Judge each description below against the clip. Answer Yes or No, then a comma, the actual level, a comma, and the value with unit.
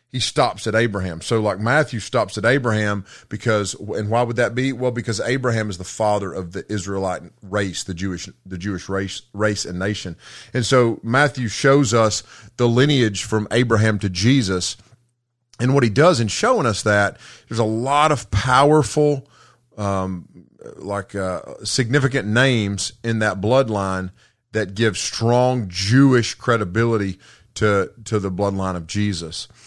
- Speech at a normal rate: Yes, average, 155 wpm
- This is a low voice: Yes, low, 110 Hz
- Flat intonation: No, average, 3.5 semitones